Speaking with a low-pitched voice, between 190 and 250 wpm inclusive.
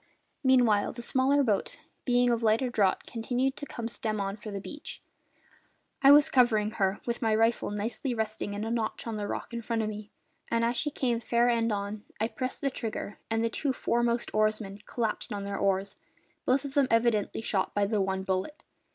No: high, 225 Hz; fast, 205 wpm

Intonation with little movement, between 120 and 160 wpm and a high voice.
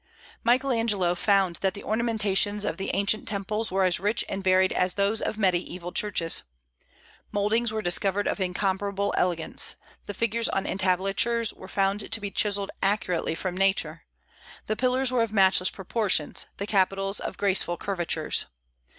Yes: narrow, 2.2 semitones; average, 155 wpm; high, 200 Hz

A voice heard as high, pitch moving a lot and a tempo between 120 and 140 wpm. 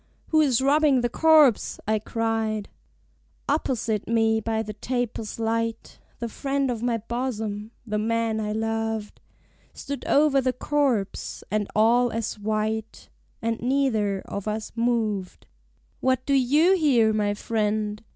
No: high, 225 Hz; average, 3.1 semitones; slow, 135 wpm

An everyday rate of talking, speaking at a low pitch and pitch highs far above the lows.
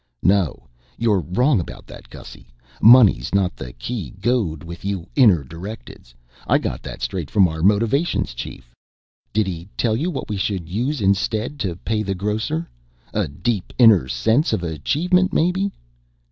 Yes: average, 160 wpm; low, 100 Hz; wide, 5.7 semitones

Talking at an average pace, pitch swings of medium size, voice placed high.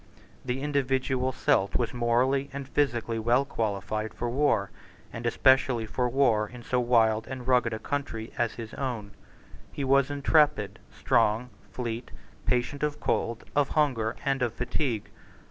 No: average, 145 wpm; average, 3.1 semitones; low, 125 Hz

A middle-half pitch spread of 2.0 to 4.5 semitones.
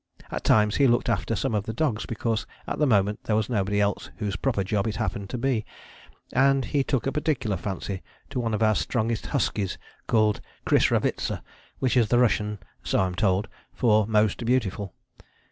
Yes: average, 3.0 semitones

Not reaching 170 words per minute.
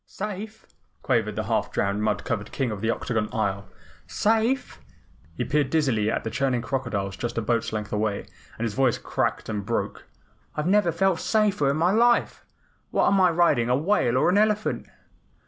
No: average, 185 wpm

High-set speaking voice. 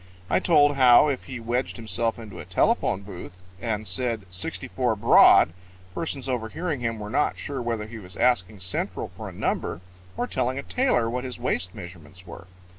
No: low, 115 Hz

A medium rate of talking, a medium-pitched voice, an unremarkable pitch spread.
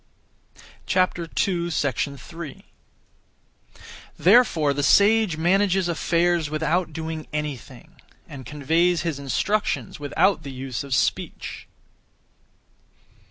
No: slow, 80 wpm; medium, 160 Hz; average, 3.8 semitones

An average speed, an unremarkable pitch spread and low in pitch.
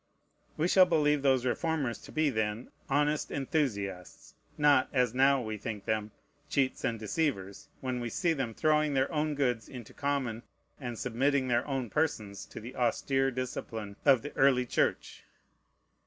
Yes: average, 155 wpm; average, 4.0 semitones; low, 130 Hz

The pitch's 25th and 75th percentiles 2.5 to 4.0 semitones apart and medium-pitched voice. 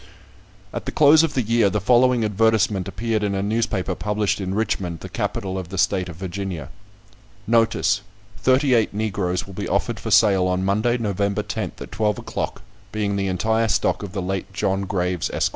No: average, 2.8 semitones; low, 100 Hz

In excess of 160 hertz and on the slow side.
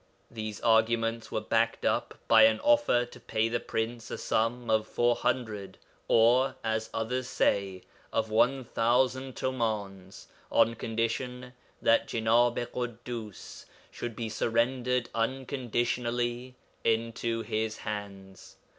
No: low, 115 Hz; slow, 115 wpm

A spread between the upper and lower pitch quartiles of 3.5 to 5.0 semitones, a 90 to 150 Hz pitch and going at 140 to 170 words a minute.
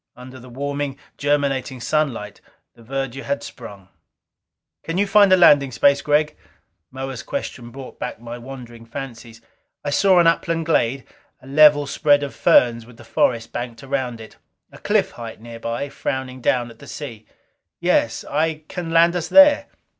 Yes: average, 4.0 semitones; low, 135 Hz; average, 160 wpm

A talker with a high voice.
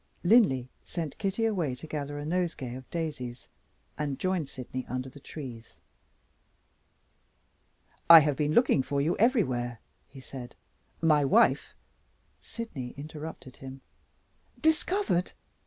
No: medium, 150 Hz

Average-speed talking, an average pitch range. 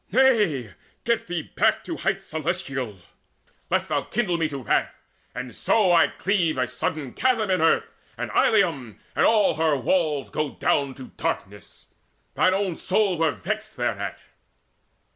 No: average, 150 wpm; wide, 6.7 semitones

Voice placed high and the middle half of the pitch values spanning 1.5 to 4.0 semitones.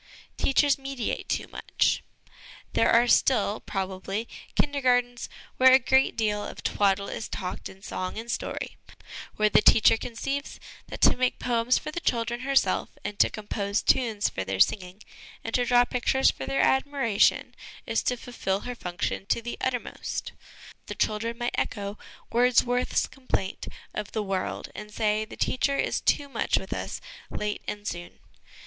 Yes: high, 230 Hz; average, 3.5 semitones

